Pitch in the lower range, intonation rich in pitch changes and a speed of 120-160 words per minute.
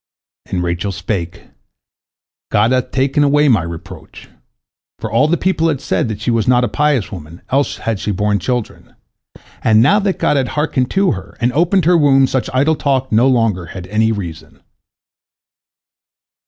No: low, 120 Hz; wide, 5.9 semitones; average, 170 wpm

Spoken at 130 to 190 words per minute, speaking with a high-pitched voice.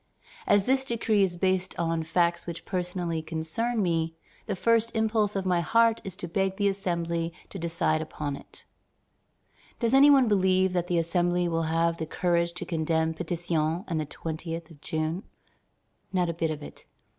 No: average, 175 wpm; medium, 175 Hz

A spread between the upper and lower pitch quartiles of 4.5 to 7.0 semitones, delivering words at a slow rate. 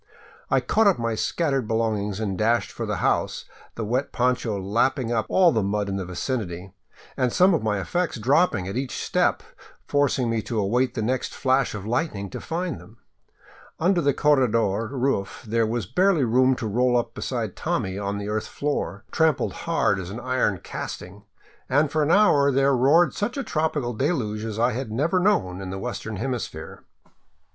No: average, 5.3 semitones; average, 185 wpm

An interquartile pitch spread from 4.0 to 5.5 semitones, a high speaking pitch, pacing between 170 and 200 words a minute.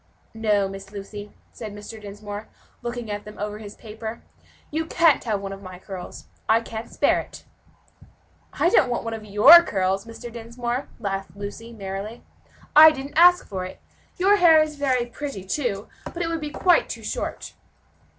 Yes: average, 5.2 semitones; high, 225 Hz; average, 175 wpm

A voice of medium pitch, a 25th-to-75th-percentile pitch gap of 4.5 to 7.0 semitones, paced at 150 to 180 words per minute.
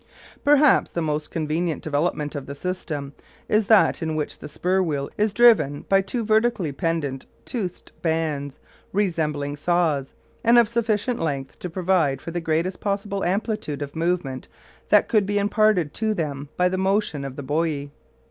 Yes: medium, 170 Hz; wide, 5.6 semitones; average, 165 wpm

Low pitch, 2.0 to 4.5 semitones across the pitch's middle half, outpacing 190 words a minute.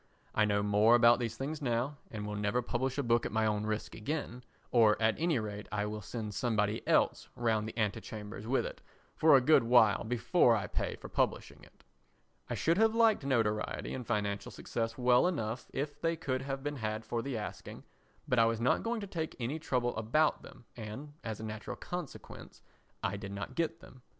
Yes: low, 115 Hz; average, 4.1 semitones; fast, 205 wpm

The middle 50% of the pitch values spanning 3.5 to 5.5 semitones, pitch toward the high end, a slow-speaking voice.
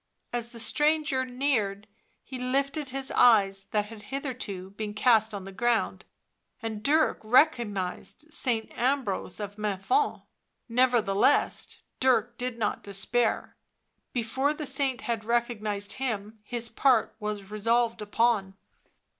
Yes: average, 3.8 semitones; high, 230 Hz; slow, 125 wpm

